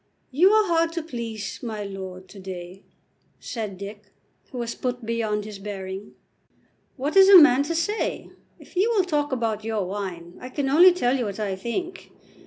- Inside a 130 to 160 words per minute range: No, average, 185 wpm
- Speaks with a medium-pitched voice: No, high, 230 Hz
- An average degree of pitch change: No, wide, 7.8 semitones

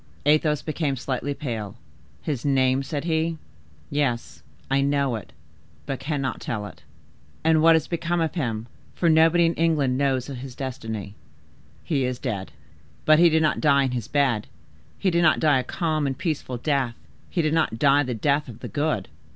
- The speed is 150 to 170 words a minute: No, average, 180 wpm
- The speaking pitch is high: No, medium, 140 Hz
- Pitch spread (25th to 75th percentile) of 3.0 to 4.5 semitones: Yes, average, 3.7 semitones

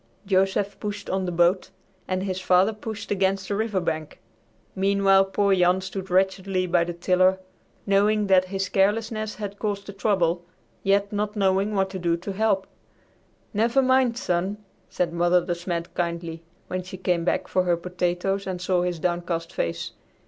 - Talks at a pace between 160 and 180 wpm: Yes, average, 170 wpm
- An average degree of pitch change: No, narrow, 2.1 semitones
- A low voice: No, high, 190 Hz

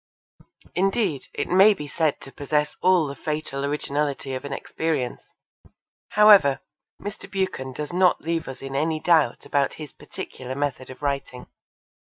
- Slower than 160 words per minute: Yes, average, 145 wpm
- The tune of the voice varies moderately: Yes, average, 4.0 semitones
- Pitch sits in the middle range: Yes, medium, 150 Hz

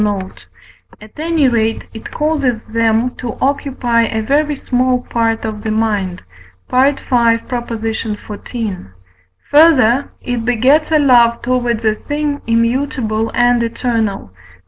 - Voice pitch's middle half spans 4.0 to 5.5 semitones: No, average, 2.8 semitones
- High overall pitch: Yes, high, 235 Hz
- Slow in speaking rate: Yes, slow, 125 wpm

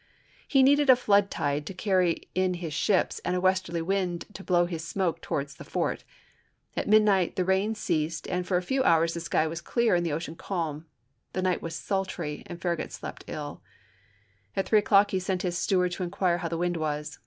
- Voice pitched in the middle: Yes, medium, 180 Hz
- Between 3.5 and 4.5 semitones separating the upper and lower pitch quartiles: No, narrow, 2.6 semitones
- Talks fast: Yes, fast, 210 wpm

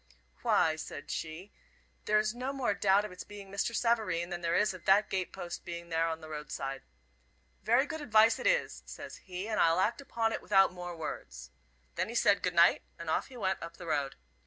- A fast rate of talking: Yes, fast, 220 wpm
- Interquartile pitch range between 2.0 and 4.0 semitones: No, average, 4.4 semitones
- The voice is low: No, high, 190 Hz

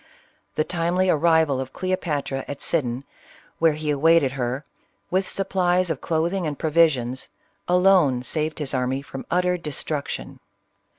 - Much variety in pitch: No, average, 4.4 semitones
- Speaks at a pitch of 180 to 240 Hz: No, medium, 155 Hz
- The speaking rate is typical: No, slow, 130 wpm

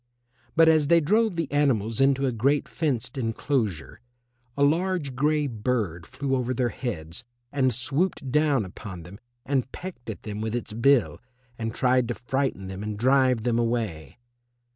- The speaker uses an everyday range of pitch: Yes, average, 4.5 semitones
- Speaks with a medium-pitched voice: No, low, 125 Hz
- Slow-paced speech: No, average, 165 wpm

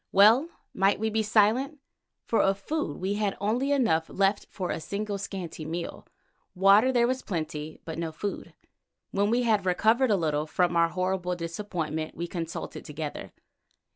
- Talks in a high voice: Yes, high, 195 Hz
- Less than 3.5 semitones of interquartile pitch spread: No, average, 4.4 semitones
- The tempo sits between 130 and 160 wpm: No, average, 170 wpm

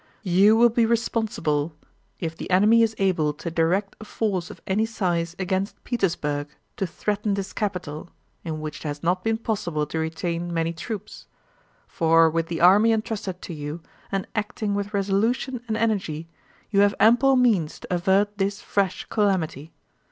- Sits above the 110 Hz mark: Yes, high, 190 Hz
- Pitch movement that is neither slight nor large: Yes, average, 4.4 semitones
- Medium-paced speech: Yes, average, 165 wpm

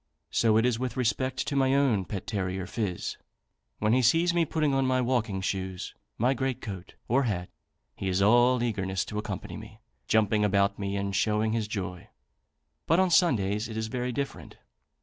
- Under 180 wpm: No, average, 185 wpm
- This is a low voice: Yes, low, 110 Hz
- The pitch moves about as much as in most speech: Yes, average, 4.5 semitones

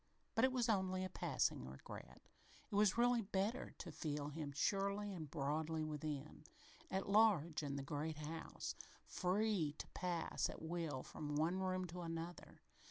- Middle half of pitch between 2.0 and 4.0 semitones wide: No, average, 4.4 semitones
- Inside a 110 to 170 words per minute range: Yes, average, 160 wpm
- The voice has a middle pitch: Yes, medium, 170 Hz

